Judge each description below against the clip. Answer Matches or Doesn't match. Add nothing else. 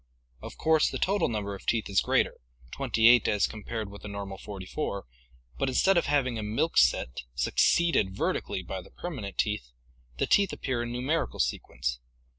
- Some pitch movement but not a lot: Doesn't match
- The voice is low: Matches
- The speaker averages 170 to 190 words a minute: Matches